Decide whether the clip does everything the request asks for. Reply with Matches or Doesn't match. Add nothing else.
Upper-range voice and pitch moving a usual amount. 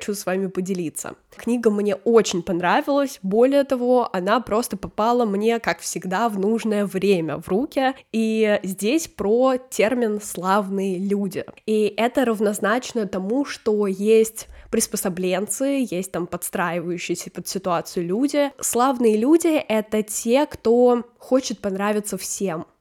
Matches